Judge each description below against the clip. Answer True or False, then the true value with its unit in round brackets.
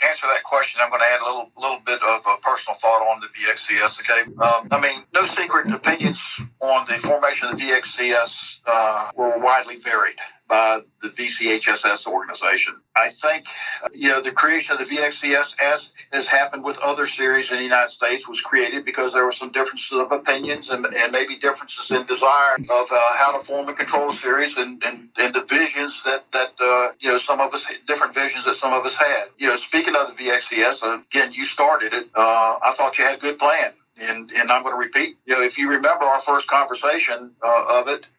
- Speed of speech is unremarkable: False (215 wpm)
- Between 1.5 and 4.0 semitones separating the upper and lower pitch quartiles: True (2.9 semitones)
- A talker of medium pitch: False (130 Hz)